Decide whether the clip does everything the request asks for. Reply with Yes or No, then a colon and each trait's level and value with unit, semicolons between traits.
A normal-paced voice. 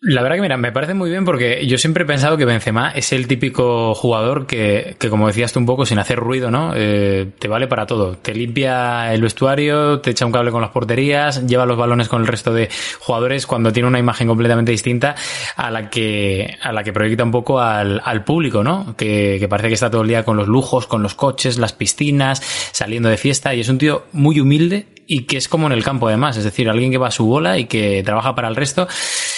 No: fast, 245 wpm